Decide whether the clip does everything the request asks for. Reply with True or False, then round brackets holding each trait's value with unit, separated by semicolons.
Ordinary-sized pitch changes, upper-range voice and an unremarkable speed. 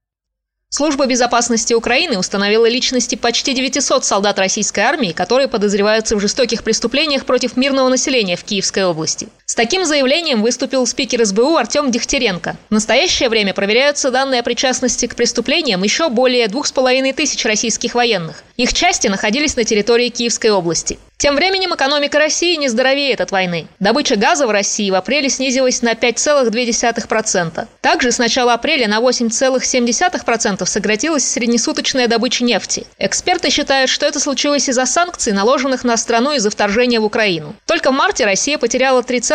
True (3.4 semitones; 245 Hz; 150 wpm)